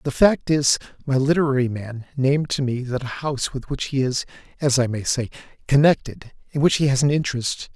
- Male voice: Yes, male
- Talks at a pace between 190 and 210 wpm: Yes, average, 200 wpm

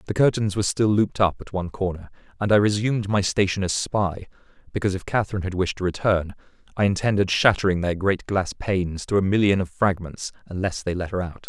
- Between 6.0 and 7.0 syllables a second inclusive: Yes, 6.2 syllables/s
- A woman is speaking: No, male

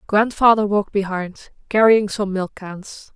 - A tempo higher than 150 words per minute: No, slow, 135 wpm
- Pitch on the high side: Yes, high, 205 Hz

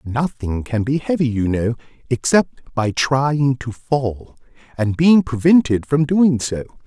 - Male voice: Yes, male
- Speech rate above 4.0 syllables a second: No, 3.8 syllables/s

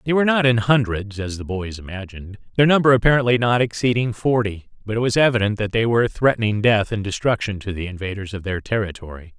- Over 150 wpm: Yes, fast, 205 wpm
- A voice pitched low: Yes, low, 110 Hz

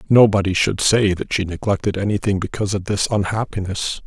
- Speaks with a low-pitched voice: Yes, low, 100 Hz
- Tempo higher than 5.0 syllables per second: Yes, 5.8 syllables/s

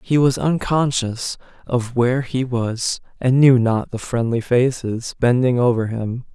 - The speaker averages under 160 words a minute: Yes, average, 150 wpm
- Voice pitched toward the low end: Yes, low, 125 Hz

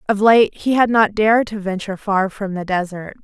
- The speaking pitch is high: Yes, high, 205 Hz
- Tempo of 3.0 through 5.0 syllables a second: No, 5.3 syllables/s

